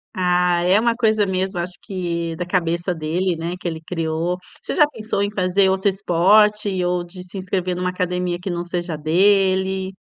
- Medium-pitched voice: Yes, medium, 180 Hz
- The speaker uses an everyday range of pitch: No, narrow, 1.8 semitones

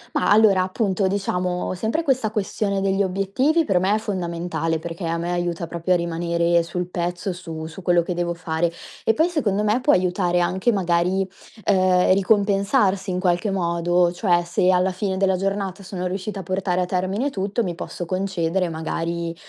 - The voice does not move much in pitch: Yes, narrow, 2.3 semitones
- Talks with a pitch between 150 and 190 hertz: Yes, medium, 185 Hz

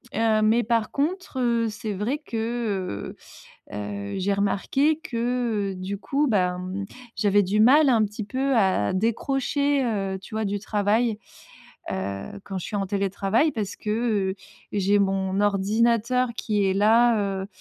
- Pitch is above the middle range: Yes, high, 210 Hz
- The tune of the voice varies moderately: Yes, average, 3.4 semitones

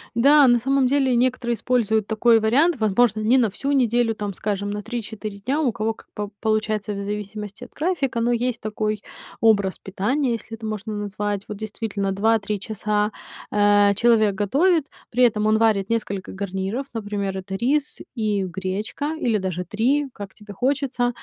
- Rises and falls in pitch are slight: No, average, 3.0 semitones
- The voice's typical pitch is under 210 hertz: No, high, 220 Hz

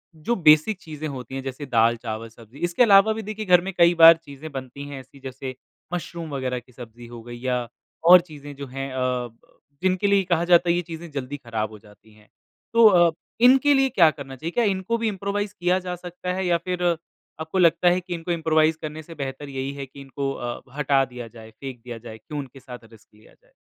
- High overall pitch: No, medium, 150 Hz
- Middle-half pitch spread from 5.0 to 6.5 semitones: Yes, wide, 5.5 semitones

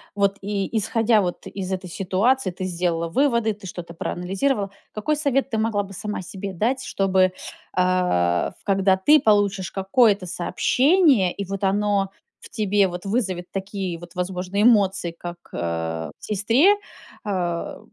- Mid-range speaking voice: No, high, 195 Hz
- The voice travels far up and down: No, average, 2.9 semitones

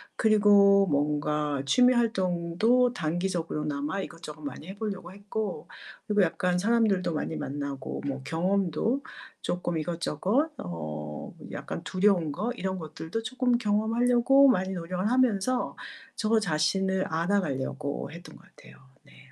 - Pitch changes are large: Yes, wide, 5.8 semitones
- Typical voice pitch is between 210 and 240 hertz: No, medium, 185 Hz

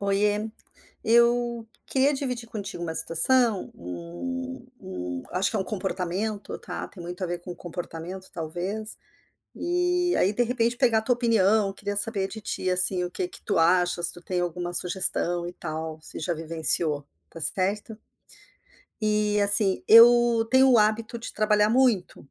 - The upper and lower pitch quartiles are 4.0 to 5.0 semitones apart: Yes, average, 4.6 semitones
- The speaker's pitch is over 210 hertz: No, high, 200 Hz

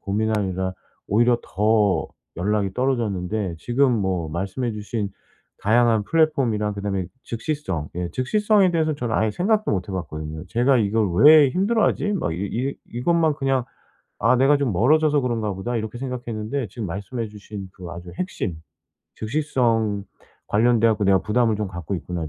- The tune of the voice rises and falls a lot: No, average, 4.9 semitones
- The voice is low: Yes, low, 110 Hz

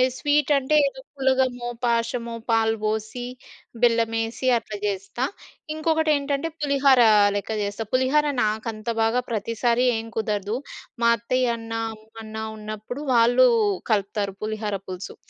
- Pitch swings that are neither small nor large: Yes, average, 3.1 semitones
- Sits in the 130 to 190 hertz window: No, high, 230 Hz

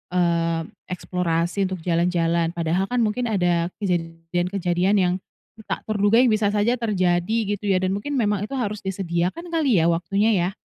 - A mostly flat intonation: No, average, 3.5 semitones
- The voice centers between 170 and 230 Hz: Yes, medium, 185 Hz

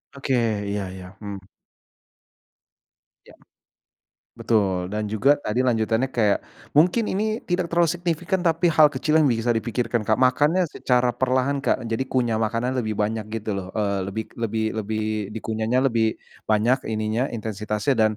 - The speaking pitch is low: Yes, low, 115 Hz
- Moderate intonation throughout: Yes, average, 4.4 semitones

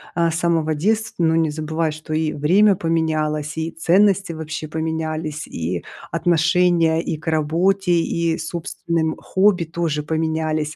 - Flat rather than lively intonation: Yes, narrow, 1.6 semitones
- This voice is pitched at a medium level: Yes, medium, 160 Hz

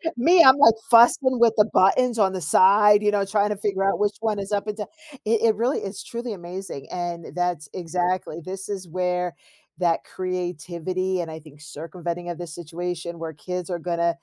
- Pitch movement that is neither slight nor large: Yes, average, 3.2 semitones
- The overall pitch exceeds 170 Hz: Yes, medium, 185 Hz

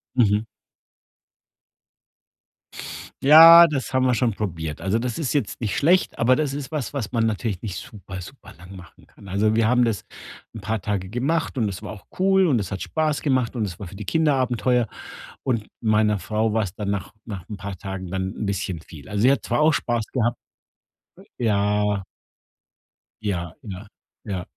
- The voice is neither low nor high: No, low, 110 Hz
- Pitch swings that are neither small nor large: Yes, average, 4.5 semitones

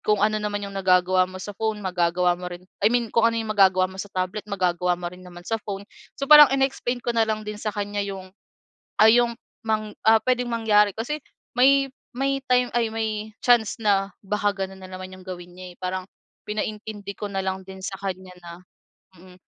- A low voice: No, high, 205 Hz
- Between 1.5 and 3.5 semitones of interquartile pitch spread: Yes, average, 3.1 semitones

